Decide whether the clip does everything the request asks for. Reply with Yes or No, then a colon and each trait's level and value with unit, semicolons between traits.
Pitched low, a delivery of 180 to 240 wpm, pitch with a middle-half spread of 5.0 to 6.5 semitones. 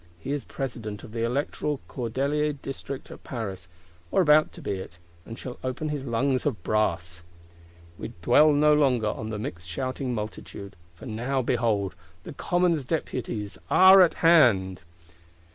No: low, 125 Hz; average, 155 wpm; wide, 5.6 semitones